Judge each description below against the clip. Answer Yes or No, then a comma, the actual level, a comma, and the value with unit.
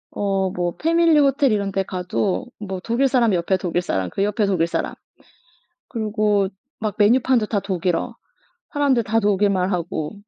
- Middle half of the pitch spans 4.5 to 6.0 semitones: No, average, 3.8 semitones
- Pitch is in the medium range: No, high, 205 Hz